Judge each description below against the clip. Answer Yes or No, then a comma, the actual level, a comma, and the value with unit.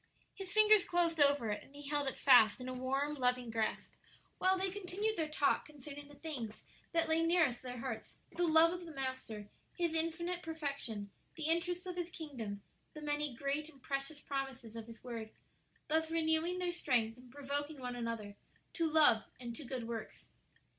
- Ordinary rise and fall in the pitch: Yes, average, 4.8 semitones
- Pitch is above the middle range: Yes, very high, 290 Hz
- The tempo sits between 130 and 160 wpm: No, average, 185 wpm